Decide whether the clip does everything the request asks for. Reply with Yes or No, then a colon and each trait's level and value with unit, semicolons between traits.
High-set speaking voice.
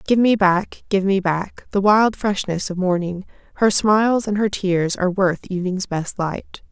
Yes: high, 195 Hz